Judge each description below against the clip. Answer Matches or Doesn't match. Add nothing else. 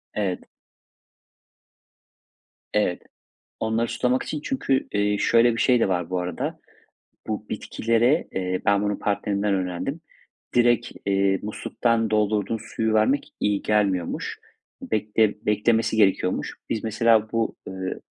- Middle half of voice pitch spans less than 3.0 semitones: Matches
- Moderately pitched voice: Doesn't match